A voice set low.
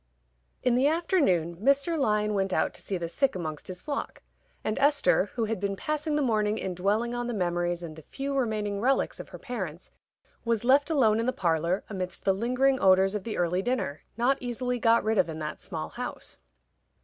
No: high, 215 Hz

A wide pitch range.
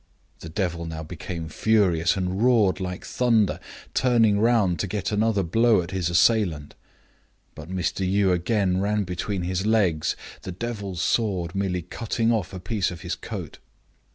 No: average, 3.5 semitones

